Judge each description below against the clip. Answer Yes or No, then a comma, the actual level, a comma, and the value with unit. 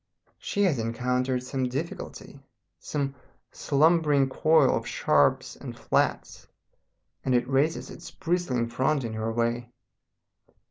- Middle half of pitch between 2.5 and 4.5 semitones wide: Yes, average, 3.9 semitones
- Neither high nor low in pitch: No, low, 130 Hz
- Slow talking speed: Yes, slow, 120 wpm